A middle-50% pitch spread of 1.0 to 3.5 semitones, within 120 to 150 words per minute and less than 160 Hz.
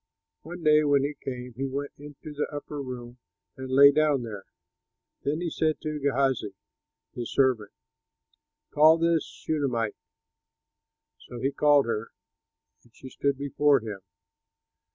Yes: average, 3.1 semitones; slow, 135 wpm; medium, 140 Hz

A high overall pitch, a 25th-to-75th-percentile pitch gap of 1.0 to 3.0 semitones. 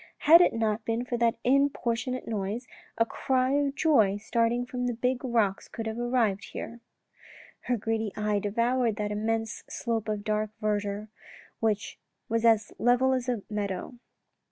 Yes: high, 230 Hz; average, 2.7 semitones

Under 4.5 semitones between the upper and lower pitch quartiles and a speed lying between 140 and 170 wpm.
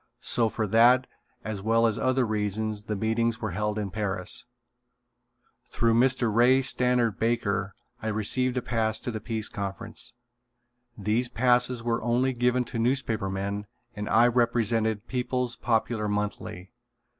Yes: narrow, 2.5 semitones; average, 145 wpm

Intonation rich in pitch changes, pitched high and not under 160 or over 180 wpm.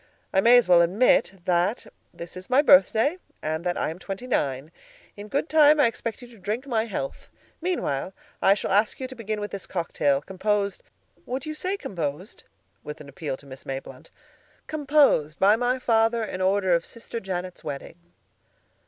Yes: wide, 6.2 semitones; high, 200 Hz; average, 175 wpm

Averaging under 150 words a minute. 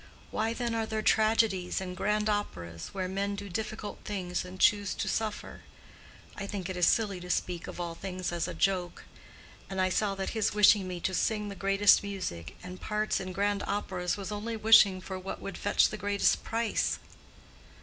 No: average, 190 wpm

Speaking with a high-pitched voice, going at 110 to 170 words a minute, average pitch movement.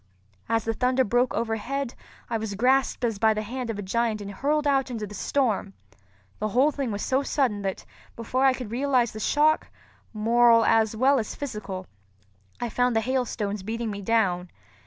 No: high, 230 Hz; average, 185 wpm; average, 3.4 semitones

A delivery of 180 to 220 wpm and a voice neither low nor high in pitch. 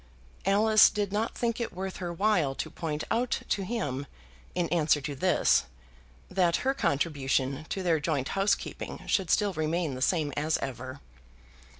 No: average, 160 wpm; medium, 170 Hz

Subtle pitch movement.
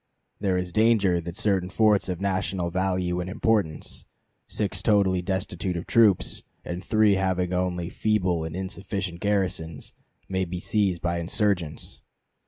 Yes: narrow, 2.1 semitones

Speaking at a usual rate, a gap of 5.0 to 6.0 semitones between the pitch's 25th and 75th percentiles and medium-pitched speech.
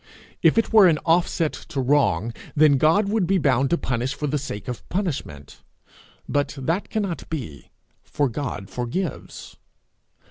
Yes: average, 155 wpm; wide, 5.4 semitones; medium, 145 Hz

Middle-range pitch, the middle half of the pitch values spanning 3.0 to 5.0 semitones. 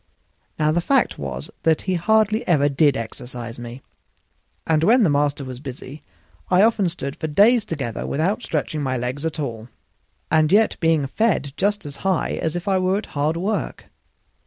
No: medium, 155 Hz; wide, 5.6 semitones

